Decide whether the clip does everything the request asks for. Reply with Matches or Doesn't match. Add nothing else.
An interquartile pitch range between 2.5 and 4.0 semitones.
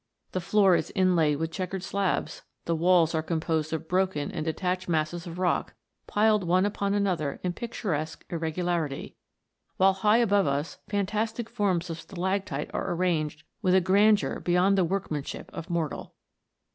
Matches